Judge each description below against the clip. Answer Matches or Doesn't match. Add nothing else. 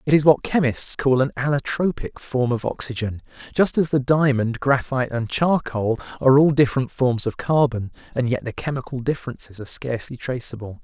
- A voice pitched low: Matches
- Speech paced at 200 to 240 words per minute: Doesn't match